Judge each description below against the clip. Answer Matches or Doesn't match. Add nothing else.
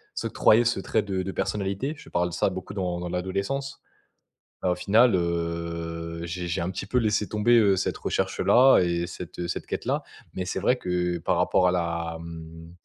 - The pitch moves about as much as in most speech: Matches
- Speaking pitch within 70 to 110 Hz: Matches